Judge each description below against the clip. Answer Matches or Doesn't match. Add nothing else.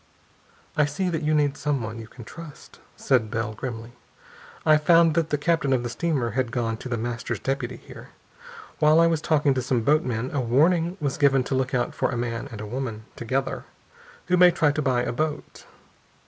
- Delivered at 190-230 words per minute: Matches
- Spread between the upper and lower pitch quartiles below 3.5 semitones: Doesn't match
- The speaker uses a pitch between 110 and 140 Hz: Matches